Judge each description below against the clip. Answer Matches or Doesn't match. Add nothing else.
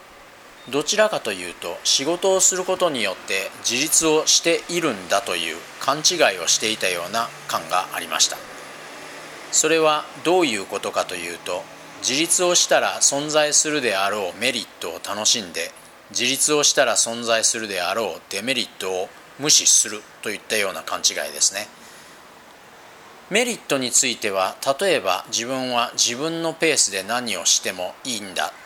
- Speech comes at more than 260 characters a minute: Matches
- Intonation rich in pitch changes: Doesn't match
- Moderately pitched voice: Matches